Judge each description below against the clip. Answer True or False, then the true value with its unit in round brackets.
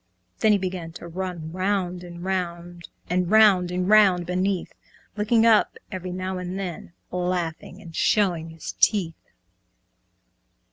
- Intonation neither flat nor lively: False (1.8 semitones)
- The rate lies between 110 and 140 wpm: True (135 wpm)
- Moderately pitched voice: True (180 Hz)